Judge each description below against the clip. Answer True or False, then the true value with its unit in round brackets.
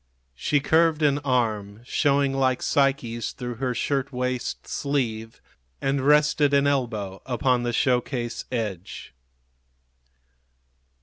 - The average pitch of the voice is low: True (130 Hz)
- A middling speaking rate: False (115 wpm)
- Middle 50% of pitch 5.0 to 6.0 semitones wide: False (3.1 semitones)